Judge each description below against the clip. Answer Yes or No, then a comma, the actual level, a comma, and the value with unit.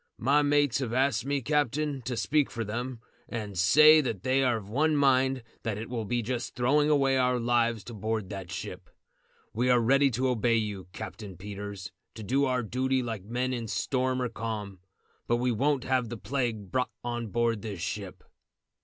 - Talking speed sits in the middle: Yes, average, 190 wpm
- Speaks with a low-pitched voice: Yes, low, 120 Hz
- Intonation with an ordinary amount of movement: Yes, average, 3.3 semitones